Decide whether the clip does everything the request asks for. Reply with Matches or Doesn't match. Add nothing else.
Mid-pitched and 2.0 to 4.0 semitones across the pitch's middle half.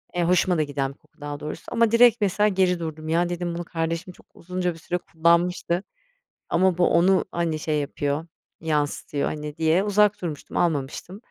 Matches